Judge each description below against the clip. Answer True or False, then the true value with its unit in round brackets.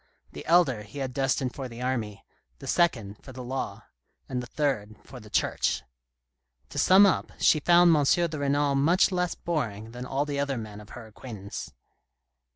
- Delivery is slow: False (180 wpm)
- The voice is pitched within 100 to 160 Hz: True (135 Hz)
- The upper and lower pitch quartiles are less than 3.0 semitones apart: False (4.7 semitones)